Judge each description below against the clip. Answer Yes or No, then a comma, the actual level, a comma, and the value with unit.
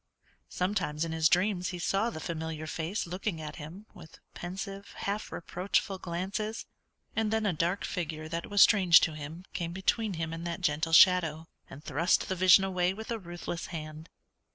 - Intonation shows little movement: No, average, 3.3 semitones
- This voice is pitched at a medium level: Yes, medium, 175 Hz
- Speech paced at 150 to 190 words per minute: Yes, average, 175 wpm